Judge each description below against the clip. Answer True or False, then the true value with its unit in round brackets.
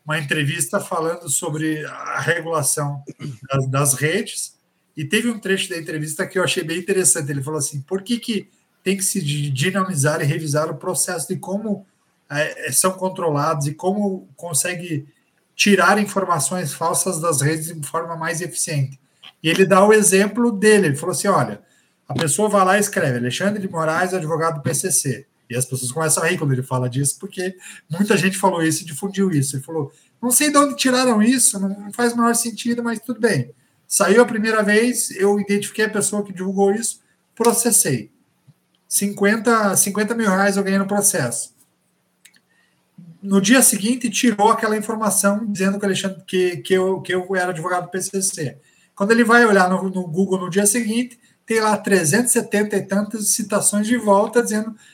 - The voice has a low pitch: False (190 Hz)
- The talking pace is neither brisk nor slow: True (175 wpm)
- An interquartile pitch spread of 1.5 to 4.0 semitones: False (4.4 semitones)